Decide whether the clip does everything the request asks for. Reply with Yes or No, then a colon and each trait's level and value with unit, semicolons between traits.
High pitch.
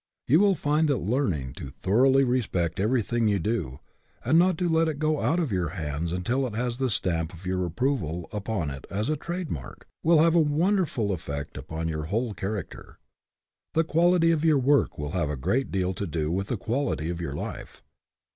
No: low, 110 Hz